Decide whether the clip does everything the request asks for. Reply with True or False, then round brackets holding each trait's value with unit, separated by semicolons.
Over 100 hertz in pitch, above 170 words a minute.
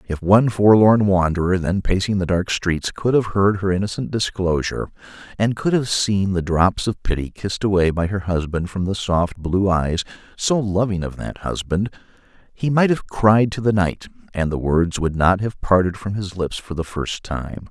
False (95 Hz; 195 wpm)